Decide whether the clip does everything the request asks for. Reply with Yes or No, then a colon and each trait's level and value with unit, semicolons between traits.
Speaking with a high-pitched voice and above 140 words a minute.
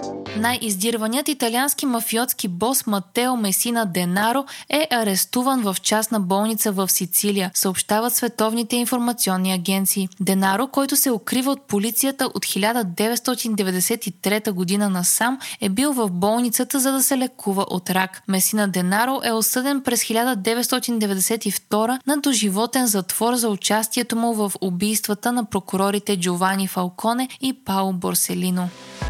No: high, 220 Hz; average, 120 wpm